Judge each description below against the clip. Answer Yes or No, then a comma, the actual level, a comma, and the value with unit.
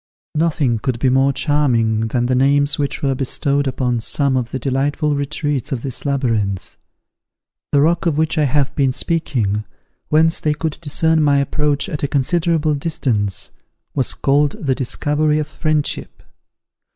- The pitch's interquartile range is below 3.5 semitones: Yes, average, 2.8 semitones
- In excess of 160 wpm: No, average, 155 wpm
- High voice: No, medium, 140 Hz